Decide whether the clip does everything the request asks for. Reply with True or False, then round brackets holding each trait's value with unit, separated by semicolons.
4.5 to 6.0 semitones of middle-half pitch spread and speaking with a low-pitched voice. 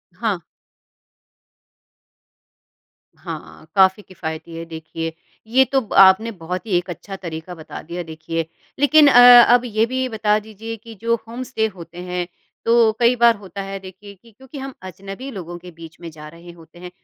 False (5.2 semitones; 195 Hz)